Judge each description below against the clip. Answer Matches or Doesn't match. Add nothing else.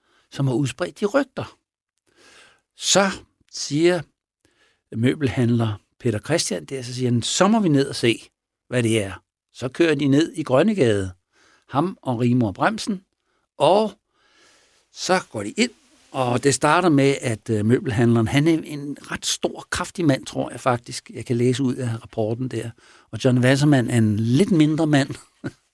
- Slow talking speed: Doesn't match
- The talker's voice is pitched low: Matches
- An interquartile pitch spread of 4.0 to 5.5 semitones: Matches